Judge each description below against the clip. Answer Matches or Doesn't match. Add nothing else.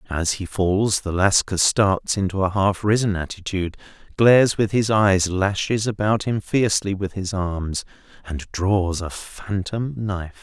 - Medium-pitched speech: Doesn't match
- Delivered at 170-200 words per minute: Doesn't match